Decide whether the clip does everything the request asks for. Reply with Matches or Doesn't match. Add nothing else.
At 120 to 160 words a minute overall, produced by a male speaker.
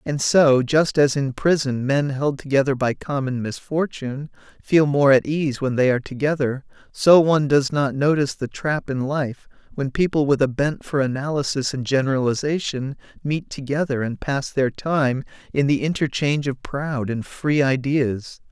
Doesn't match